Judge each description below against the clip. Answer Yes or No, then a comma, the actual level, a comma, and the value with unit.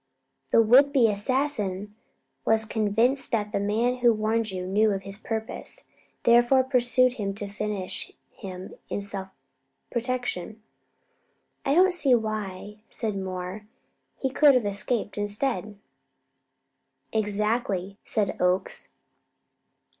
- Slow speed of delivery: Yes, slow, 120 wpm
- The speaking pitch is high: Yes, high, 215 Hz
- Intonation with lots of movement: No, average, 3.4 semitones